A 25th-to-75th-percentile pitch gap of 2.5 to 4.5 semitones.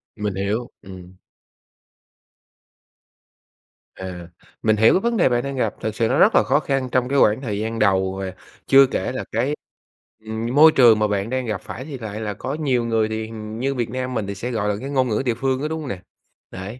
Yes: average, 3.8 semitones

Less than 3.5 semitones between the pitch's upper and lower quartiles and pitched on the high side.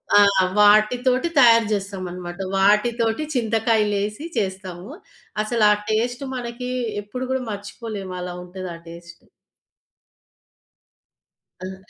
No: average, 3.8 semitones; high, 210 Hz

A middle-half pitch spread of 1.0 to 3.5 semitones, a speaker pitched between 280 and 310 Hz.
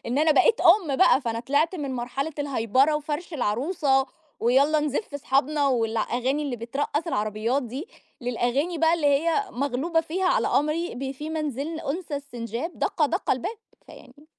No: average, 4.0 semitones; very high, 285 Hz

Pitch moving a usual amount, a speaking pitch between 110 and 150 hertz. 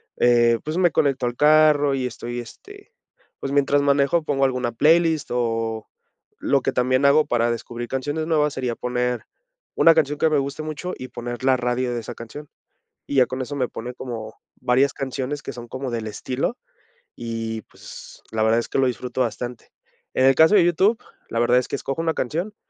Yes: average, 3.6 semitones; low, 130 Hz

